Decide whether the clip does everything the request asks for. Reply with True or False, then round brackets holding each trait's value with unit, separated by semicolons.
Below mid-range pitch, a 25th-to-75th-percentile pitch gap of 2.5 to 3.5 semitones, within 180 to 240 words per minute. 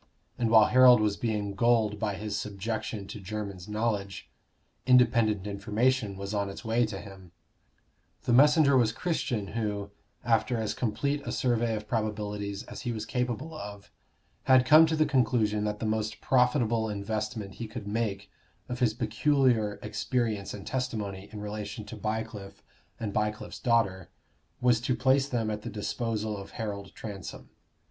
False (110 Hz; 2.8 semitones; 155 wpm)